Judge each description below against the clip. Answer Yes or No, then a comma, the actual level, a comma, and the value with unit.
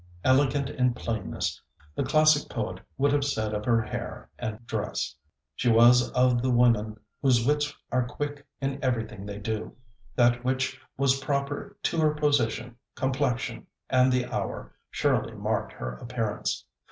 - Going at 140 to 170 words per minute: Yes, average, 150 wpm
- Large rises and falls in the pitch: No, average, 3.1 semitones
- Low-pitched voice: Yes, low, 125 Hz